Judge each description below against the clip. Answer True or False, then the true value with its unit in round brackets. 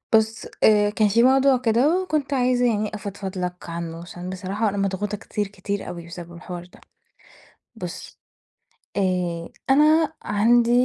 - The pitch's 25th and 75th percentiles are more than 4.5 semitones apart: True (5.0 semitones)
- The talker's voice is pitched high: True (205 Hz)